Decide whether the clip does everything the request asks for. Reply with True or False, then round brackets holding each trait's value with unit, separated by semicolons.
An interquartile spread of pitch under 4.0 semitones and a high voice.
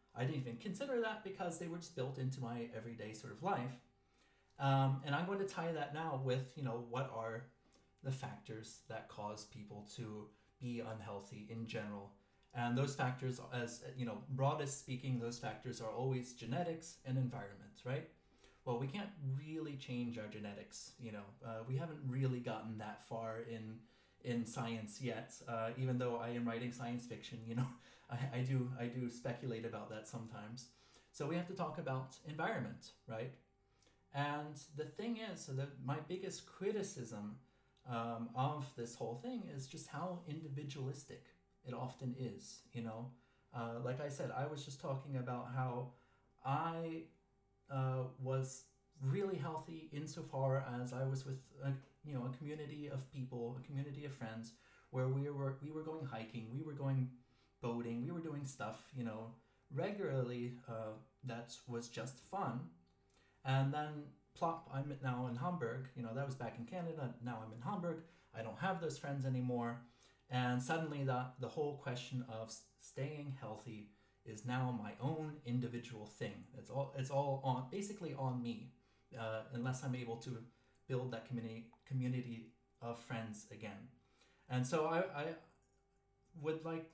False (3.3 semitones; 130 Hz)